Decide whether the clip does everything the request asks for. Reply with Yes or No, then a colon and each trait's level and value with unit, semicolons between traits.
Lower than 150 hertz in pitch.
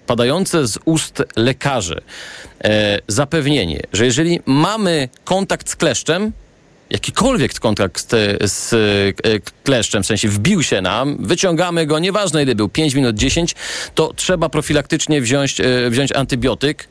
Yes: medium, 140 Hz